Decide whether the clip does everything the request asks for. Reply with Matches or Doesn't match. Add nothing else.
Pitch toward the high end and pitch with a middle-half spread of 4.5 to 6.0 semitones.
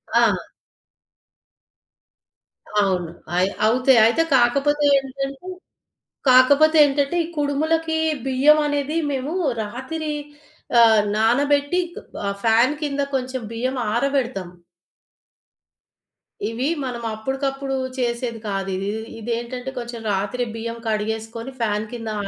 Doesn't match